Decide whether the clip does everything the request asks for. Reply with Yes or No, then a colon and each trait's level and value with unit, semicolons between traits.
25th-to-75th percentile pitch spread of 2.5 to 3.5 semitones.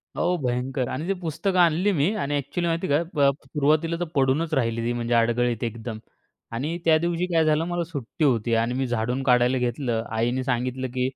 No: average, 5.2 semitones